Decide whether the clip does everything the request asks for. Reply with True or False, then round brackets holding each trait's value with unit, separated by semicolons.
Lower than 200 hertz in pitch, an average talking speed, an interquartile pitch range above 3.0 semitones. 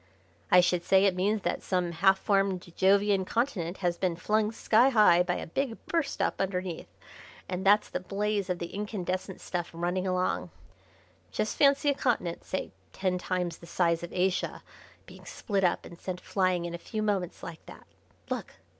False (185 Hz; 180 wpm; 2.7 semitones)